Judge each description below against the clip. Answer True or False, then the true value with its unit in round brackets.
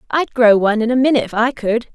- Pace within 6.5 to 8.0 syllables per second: True (7.1 syllables/s)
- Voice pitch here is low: False (235 Hz)